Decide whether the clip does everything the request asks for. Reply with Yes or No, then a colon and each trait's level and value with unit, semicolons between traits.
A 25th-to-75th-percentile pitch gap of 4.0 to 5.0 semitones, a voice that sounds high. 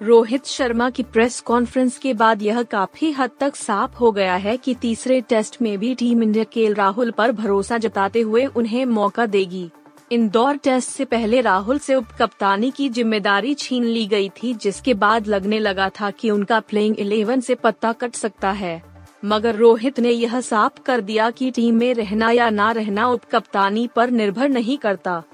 No: average, 3.0 semitones; high, 230 Hz